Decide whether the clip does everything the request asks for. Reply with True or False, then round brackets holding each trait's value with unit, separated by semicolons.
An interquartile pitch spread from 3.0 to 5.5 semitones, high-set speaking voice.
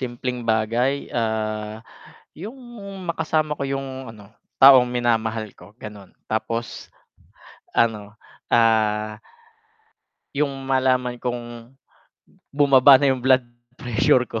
False (3.3 semitones; 120 Hz)